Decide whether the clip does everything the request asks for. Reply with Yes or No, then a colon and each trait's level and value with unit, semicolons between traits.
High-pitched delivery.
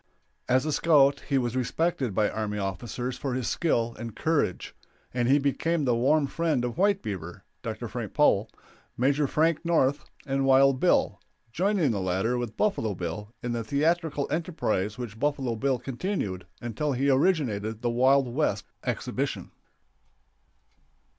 No: low, 130 Hz